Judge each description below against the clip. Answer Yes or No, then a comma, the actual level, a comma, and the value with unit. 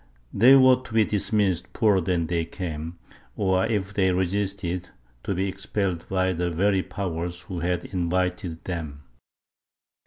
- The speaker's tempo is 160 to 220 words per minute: No, average, 145 wpm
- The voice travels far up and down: No, narrow, 2.4 semitones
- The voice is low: Yes, very low, 95 Hz